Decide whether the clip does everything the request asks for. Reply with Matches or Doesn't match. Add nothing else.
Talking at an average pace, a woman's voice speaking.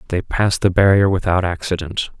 Doesn't match